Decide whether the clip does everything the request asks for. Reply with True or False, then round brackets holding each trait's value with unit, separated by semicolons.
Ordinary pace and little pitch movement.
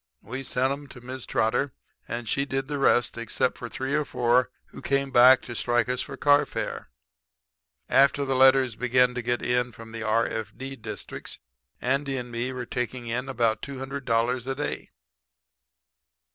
True (165 wpm; 2.1 semitones)